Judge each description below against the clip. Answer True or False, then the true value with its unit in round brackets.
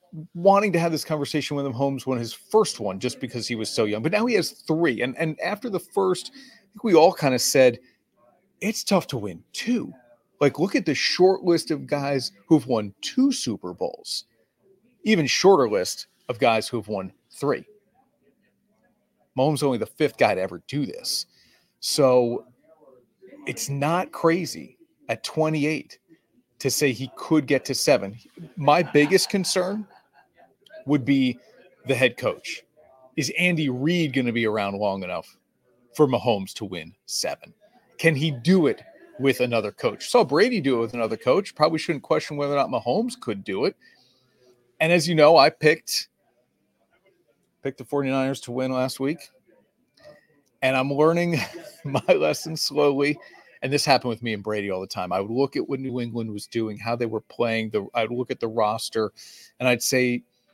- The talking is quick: False (180 wpm)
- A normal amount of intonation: False (6.1 semitones)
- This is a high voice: False (140 Hz)